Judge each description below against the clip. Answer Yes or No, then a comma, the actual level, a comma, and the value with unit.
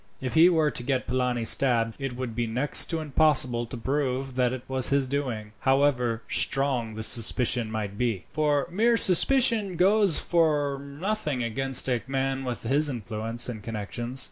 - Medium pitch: No, low, 130 Hz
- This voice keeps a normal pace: Yes, average, 170 wpm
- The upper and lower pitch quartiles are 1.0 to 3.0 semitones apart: No, average, 3.7 semitones